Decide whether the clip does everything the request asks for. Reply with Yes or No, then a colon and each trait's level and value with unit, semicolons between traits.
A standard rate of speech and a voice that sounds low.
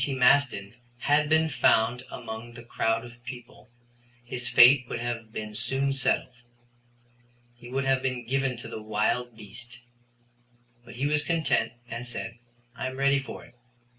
Yes: average, 160 wpm; low, 125 Hz